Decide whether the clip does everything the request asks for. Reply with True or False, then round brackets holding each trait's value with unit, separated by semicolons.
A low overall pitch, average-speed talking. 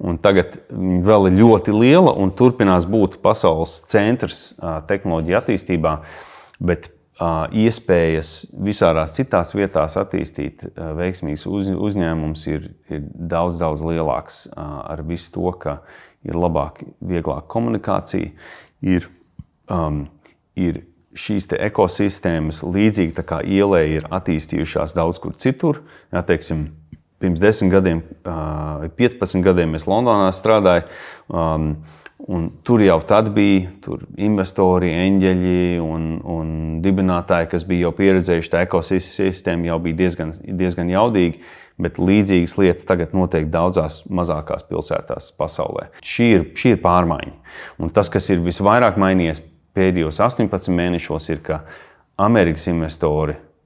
False (90 Hz; 120 wpm)